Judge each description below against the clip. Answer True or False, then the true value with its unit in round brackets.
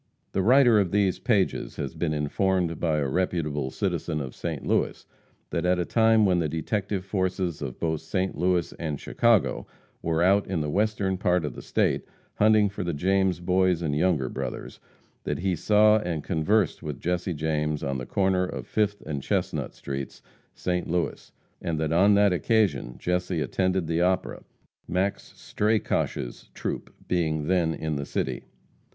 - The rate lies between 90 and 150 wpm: False (170 wpm)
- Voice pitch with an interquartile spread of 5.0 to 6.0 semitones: False (3.8 semitones)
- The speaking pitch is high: False (90 Hz)